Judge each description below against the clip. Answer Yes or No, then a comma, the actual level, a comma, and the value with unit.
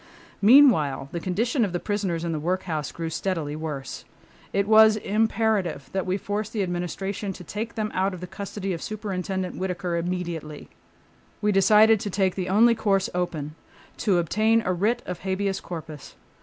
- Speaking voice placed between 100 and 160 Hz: No, high, 190 Hz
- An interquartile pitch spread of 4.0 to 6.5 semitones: No, average, 3.4 semitones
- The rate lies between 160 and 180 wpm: Yes, average, 165 wpm